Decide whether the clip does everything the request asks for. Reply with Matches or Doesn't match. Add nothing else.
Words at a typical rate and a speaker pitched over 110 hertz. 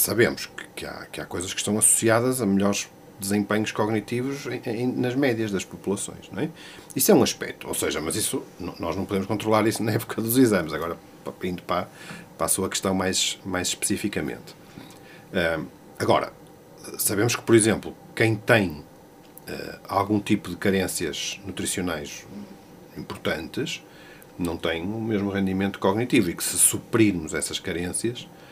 Doesn't match